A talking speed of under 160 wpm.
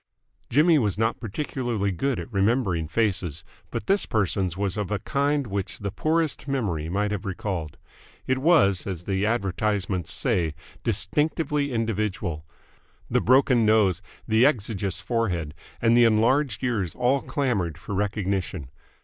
Yes: average, 140 wpm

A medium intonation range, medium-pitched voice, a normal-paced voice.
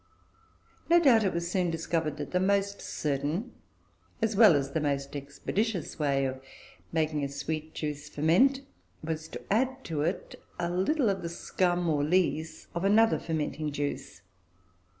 Yes: average, 4.9 semitones; medium, 165 Hz; average, 155 wpm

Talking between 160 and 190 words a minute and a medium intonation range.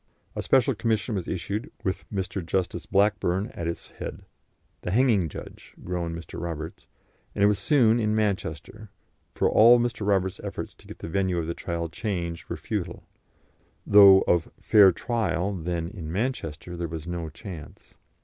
Yes: average, 165 wpm; average, 4.0 semitones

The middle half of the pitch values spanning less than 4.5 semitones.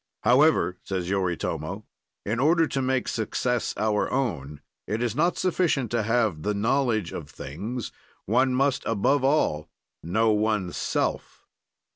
No: average, 5.2 semitones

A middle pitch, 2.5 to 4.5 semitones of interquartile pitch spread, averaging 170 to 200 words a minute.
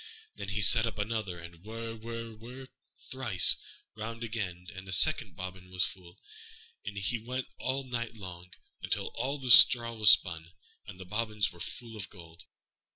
No: low, 110 Hz; average, 4.1 semitones; average, 175 wpm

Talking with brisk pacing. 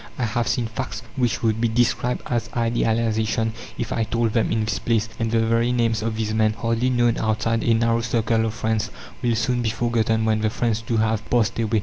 Yes: fast, 220 wpm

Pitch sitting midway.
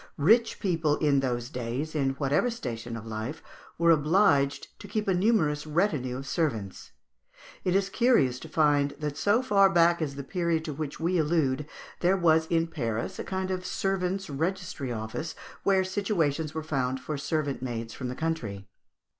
Yes: medium, 155 Hz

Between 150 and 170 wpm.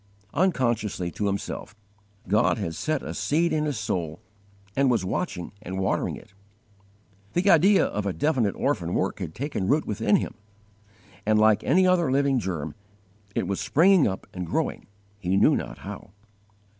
Yes: average, 160 wpm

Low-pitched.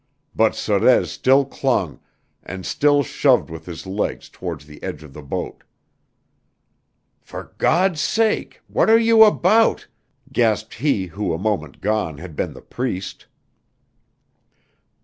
Yes: low, 110 Hz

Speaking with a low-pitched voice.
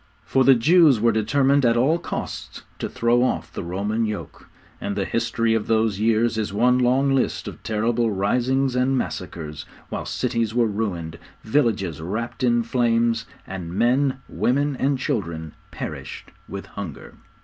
Yes: low, 115 Hz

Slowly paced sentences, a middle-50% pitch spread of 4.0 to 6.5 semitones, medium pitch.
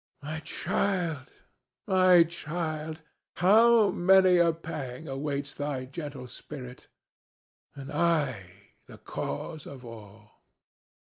Yes: slow, 95 wpm; average, 4.5 semitones; medium, 155 Hz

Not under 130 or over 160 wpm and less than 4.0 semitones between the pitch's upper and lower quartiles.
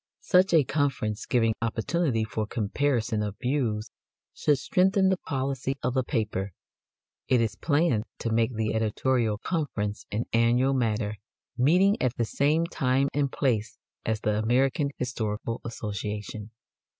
No: average, 140 wpm; average, 4.3 semitones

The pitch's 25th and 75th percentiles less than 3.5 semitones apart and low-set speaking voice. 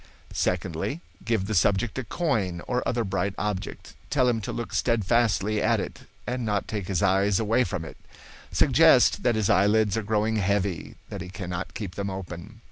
Yes: average, 3.1 semitones; low, 105 Hz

